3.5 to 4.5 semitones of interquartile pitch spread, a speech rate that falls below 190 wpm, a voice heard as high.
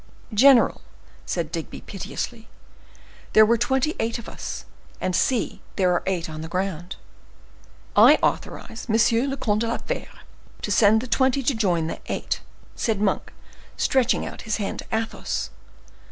Yes: average, 4.0 semitones; average, 155 wpm; high, 220 Hz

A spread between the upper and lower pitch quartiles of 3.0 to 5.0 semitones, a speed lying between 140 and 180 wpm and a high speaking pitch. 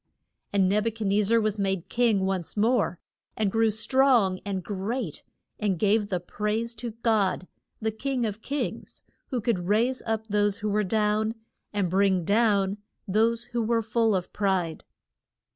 No: narrow, 2.6 semitones; average, 165 wpm; high, 210 Hz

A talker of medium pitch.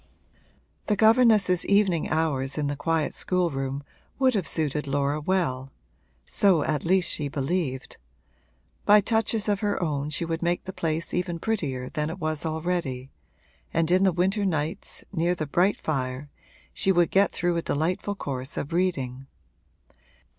Yes: medium, 165 Hz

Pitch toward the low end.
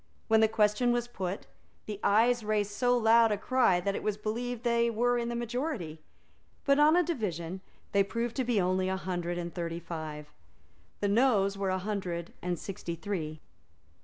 No: high, 210 Hz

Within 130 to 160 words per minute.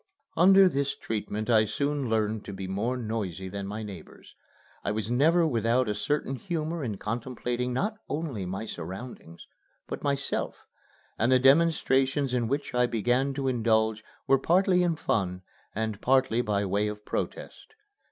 Yes: average, 155 wpm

